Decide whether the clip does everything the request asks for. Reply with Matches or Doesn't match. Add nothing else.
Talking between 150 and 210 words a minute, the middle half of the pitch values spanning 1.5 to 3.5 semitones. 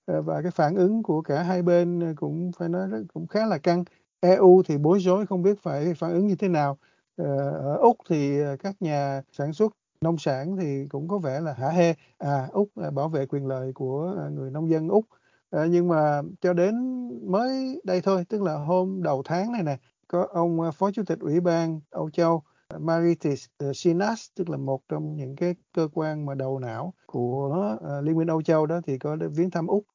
Doesn't match